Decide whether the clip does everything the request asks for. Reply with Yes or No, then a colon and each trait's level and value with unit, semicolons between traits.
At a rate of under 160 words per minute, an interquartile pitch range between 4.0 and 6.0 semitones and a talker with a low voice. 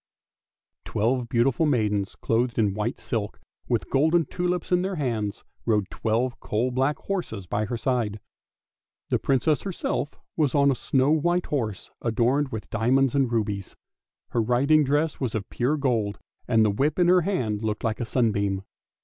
No: average, 165 wpm; average, 5.0 semitones; low, 125 Hz